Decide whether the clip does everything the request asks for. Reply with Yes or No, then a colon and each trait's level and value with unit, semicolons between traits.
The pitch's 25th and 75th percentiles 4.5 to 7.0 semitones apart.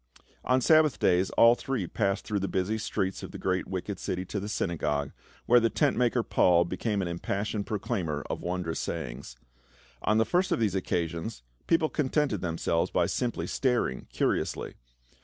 Yes: average, 5.1 semitones